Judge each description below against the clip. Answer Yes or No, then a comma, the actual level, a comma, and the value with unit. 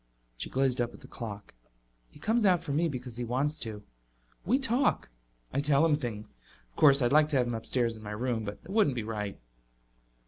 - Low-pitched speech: Yes, low, 125 Hz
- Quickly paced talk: Yes, fast, 215 wpm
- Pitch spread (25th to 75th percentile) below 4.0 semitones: No, average, 5.3 semitones